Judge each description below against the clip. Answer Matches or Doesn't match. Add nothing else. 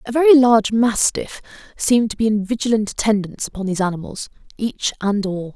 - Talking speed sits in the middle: Matches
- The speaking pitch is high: Matches